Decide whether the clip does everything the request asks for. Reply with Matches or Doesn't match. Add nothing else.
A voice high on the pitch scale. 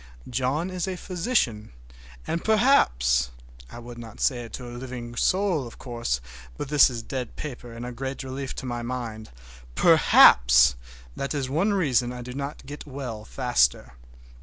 Doesn't match